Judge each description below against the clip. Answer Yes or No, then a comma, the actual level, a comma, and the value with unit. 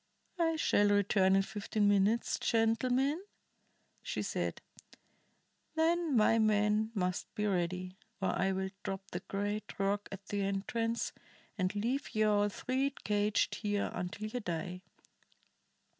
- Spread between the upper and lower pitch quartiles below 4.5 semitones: Yes, average, 2.7 semitones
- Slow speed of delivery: Yes, slow, 130 wpm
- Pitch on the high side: Yes, high, 205 Hz